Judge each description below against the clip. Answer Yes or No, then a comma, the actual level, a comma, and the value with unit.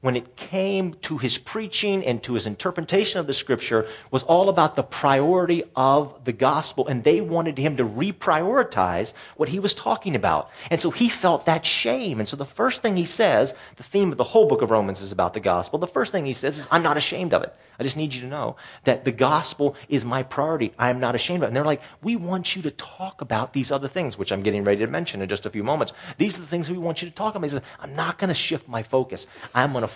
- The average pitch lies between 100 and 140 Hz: No, medium, 150 Hz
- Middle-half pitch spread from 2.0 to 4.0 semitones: No, wide, 5.5 semitones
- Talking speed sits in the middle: No, fast, 260 wpm